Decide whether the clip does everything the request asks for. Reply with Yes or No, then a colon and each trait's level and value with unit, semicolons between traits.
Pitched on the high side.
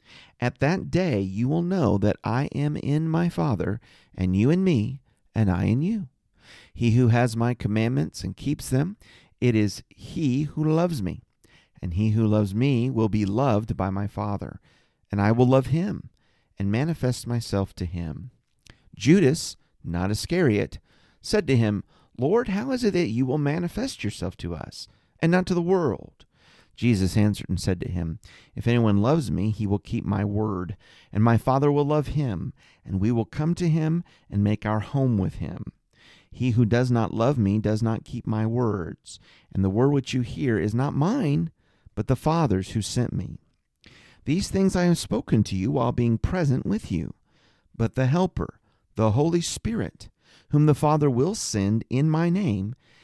No: low, 120 Hz